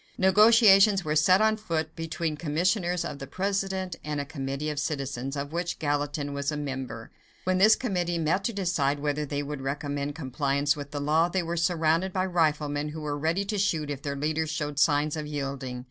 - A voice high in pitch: No, medium, 155 Hz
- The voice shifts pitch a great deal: No, average, 3.7 semitones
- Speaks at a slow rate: No, average, 195 wpm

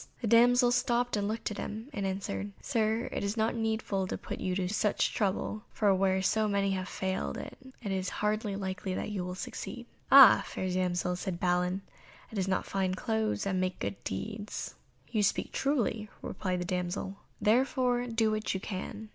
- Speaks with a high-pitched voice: Yes, high, 200 Hz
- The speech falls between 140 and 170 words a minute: No, average, 185 wpm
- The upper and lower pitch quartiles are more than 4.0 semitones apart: No, average, 2.9 semitones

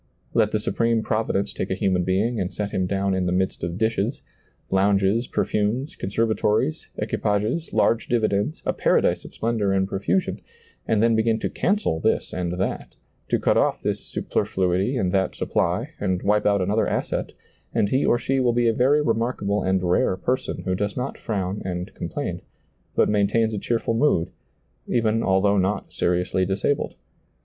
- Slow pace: No, average, 175 wpm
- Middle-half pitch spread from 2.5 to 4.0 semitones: Yes, average, 3.3 semitones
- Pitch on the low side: Yes, low, 105 Hz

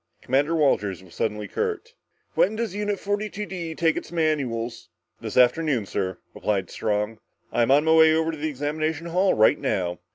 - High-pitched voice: No, medium, 155 Hz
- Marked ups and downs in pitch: Yes, wide, 7.1 semitones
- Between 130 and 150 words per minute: No, average, 170 wpm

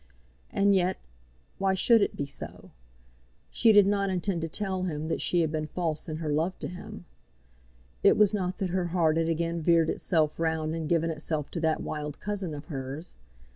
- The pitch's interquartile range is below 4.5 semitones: Yes, average, 3.2 semitones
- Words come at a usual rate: Yes, average, 195 wpm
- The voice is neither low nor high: Yes, medium, 170 Hz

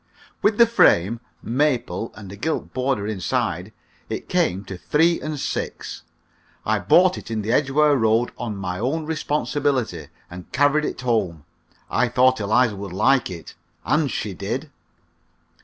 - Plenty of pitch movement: Yes, wide, 6.2 semitones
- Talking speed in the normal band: Yes, average, 150 wpm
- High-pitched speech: No, low, 120 Hz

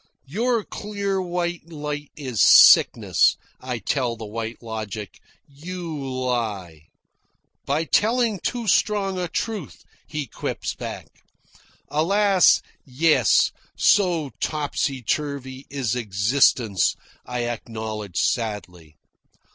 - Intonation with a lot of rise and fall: Yes, wide, 7.5 semitones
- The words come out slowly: Yes, slow, 100 wpm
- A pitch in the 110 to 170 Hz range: Yes, medium, 140 Hz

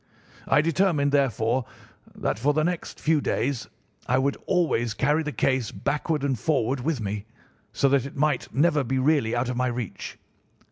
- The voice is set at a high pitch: No, medium, 140 Hz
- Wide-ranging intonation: No, average, 3.5 semitones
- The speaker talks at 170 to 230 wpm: Yes, average, 175 wpm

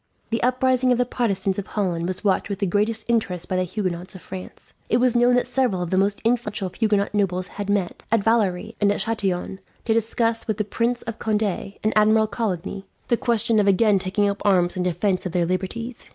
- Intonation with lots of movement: No, average, 3.4 semitones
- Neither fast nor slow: No, fast, 215 wpm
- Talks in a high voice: Yes, high, 205 Hz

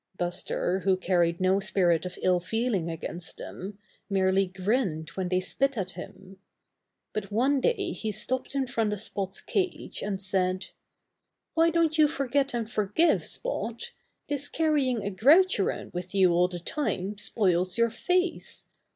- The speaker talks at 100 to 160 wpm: Yes, average, 155 wpm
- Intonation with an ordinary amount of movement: No, wide, 6.4 semitones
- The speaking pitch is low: No, high, 200 Hz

